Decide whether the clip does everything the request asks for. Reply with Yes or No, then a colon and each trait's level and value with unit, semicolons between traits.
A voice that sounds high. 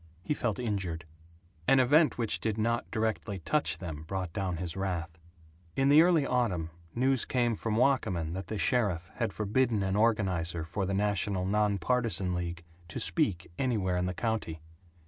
No: low, 100 Hz